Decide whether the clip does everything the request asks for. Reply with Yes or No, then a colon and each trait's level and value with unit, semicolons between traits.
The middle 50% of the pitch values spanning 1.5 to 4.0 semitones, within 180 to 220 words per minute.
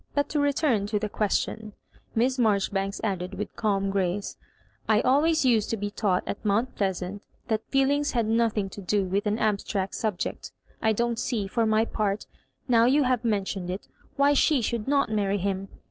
Yes: average, 3.2 semitones; average, 185 wpm